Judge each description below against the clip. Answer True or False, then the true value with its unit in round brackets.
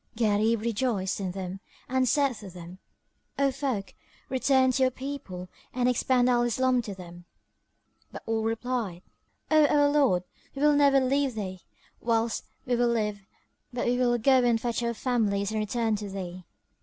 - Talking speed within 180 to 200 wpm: False (165 wpm)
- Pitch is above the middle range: True (235 Hz)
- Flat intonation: False (4.2 semitones)